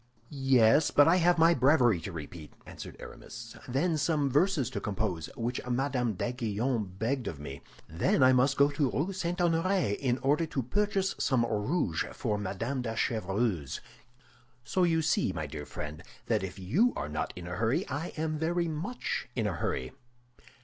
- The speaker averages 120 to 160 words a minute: No, average, 175 wpm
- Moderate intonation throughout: No, wide, 7.6 semitones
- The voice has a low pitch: Yes, low, 125 Hz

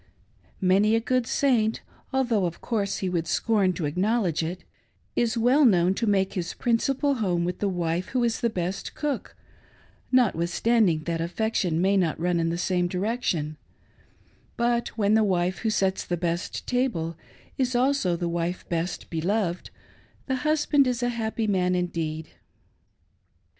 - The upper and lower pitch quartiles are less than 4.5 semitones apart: No, average, 5.3 semitones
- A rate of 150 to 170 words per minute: Yes, average, 160 wpm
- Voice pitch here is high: Yes, high, 195 Hz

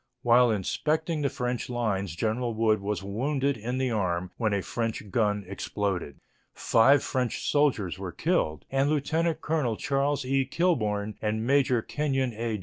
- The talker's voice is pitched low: Yes, low, 120 Hz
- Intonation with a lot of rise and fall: No, average, 4.8 semitones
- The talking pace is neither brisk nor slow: Yes, average, 150 wpm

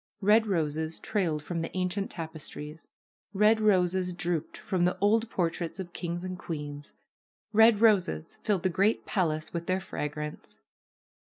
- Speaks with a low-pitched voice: No, medium, 180 Hz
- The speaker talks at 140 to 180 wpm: Yes, average, 145 wpm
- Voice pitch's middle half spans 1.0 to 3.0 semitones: No, average, 3.5 semitones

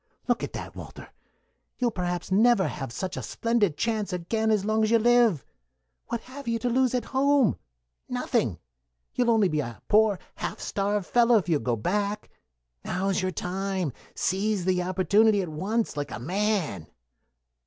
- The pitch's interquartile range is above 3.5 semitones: Yes, average, 4.2 semitones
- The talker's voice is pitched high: Yes, high, 205 Hz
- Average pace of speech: Yes, average, 165 wpm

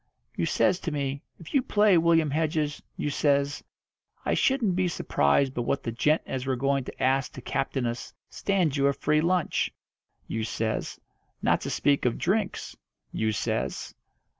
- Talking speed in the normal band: Yes, average, 170 wpm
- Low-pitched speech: No, medium, 145 Hz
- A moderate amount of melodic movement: Yes, average, 4.1 semitones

